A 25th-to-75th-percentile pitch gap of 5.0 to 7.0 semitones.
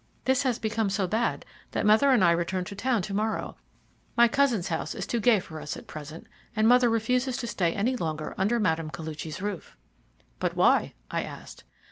Yes: wide, 5.6 semitones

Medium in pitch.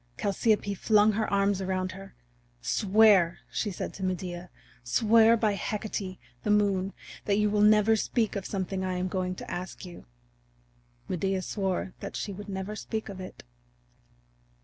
No: high, 195 Hz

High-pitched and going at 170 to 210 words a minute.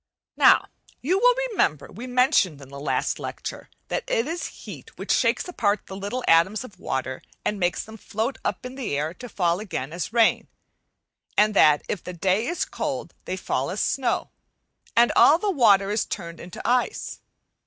Yes: high, 210 Hz; average, 185 wpm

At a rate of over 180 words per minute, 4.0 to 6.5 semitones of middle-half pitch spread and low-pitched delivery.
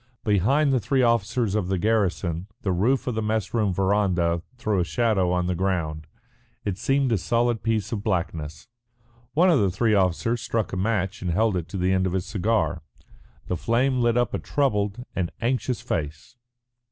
Yes: average, 190 wpm; average, 4.3 semitones; low, 105 Hz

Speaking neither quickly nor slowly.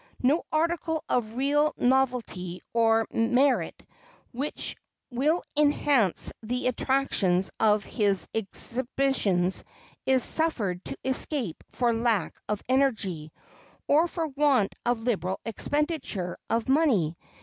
No: slow, 105 wpm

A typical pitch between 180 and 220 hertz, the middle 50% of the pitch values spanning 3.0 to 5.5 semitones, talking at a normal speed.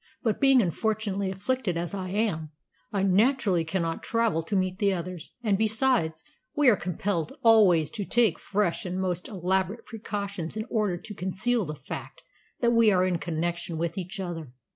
Yes: high, 190 Hz; average, 4.0 semitones; average, 170 wpm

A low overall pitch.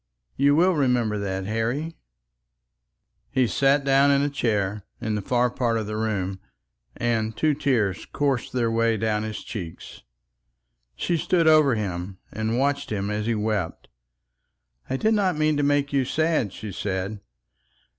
Yes: low, 115 Hz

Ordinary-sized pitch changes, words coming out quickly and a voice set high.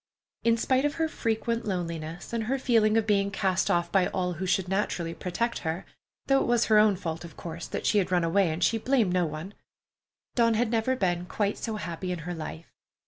Yes: average, 4.7 semitones; fast, 210 wpm; high, 195 Hz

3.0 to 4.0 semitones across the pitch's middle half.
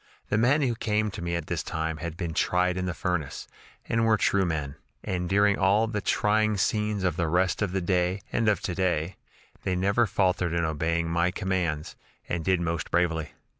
Yes: average, 3.3 semitones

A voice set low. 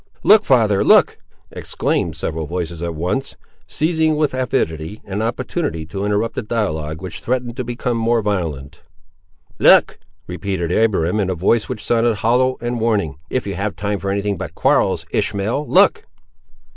Yes: low, 105 Hz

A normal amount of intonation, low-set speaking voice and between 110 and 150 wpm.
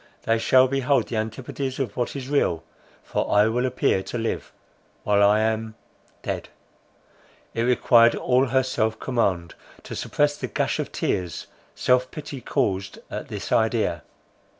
Yes: average, 3.1 semitones; low, 120 Hz; average, 140 wpm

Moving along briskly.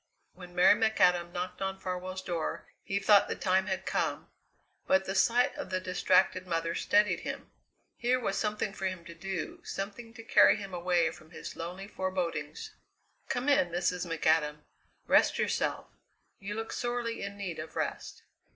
No: average, 165 wpm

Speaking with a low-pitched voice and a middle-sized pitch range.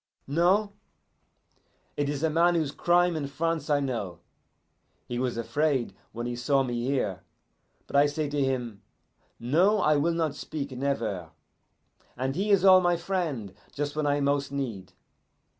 No: medium, 145 Hz; average, 4.7 semitones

